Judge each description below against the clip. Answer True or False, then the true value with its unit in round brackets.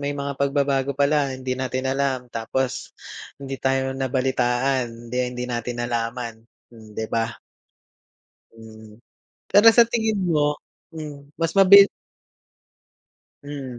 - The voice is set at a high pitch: False (130 Hz)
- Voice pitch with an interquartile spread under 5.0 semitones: True (2.6 semitones)